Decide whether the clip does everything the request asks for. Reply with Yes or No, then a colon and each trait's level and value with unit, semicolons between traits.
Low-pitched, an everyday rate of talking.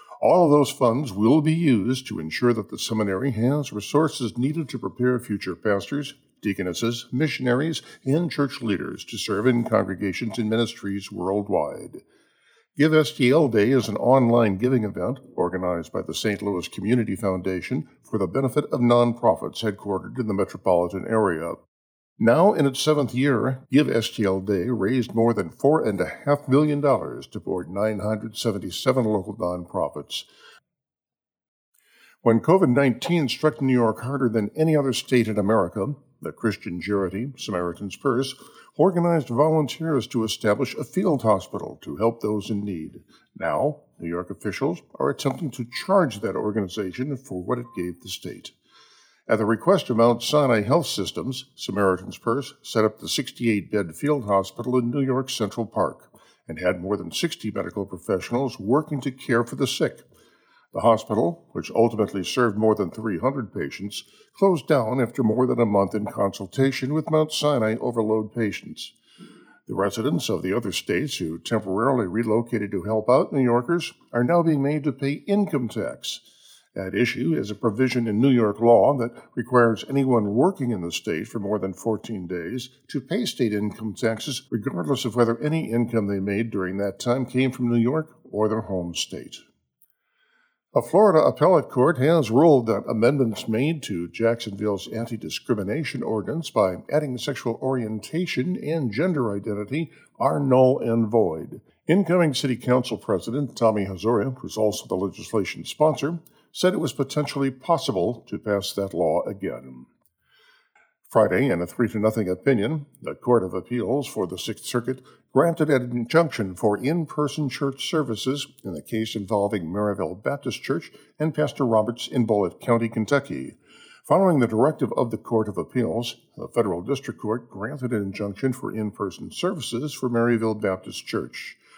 Yes: low, 120 Hz; average, 160 wpm